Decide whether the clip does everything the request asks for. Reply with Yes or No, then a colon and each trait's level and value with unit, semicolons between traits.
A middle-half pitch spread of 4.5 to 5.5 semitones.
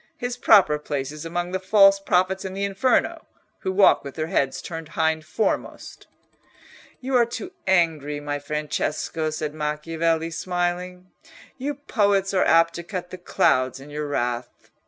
No: average, 4.0 semitones